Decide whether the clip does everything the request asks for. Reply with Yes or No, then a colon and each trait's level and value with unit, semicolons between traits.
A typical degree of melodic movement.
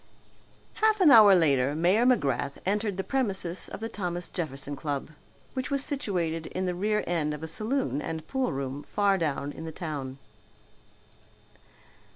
No: wide, 6.2 semitones